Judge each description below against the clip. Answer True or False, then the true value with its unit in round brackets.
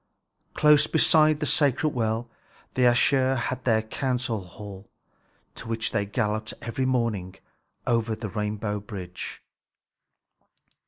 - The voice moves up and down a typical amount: True (3.6 semitones)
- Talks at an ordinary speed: False (115 wpm)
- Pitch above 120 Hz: False (115 Hz)